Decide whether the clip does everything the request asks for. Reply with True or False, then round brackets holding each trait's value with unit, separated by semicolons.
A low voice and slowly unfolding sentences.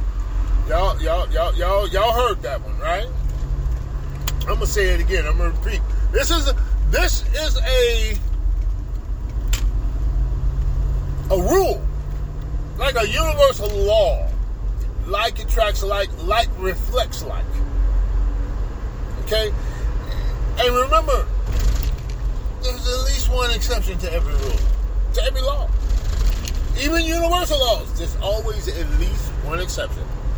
True (95 Hz; 115 wpm)